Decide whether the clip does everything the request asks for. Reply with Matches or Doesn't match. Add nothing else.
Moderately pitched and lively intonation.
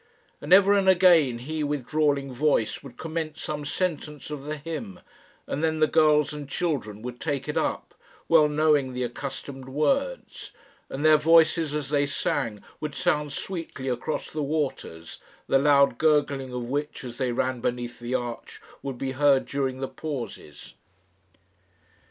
Doesn't match